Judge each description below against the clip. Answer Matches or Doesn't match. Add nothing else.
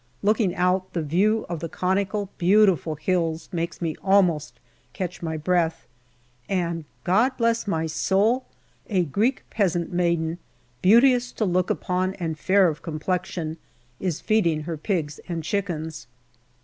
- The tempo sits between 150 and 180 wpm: Doesn't match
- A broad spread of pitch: Doesn't match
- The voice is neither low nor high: Matches